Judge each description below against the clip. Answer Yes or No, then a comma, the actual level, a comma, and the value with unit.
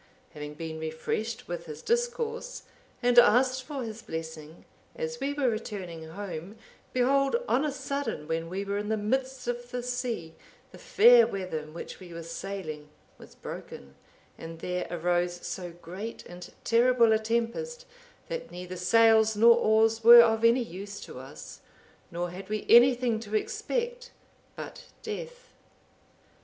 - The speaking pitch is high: Yes, high, 220 Hz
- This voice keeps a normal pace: Yes, average, 150 wpm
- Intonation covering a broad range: Yes, wide, 6.4 semitones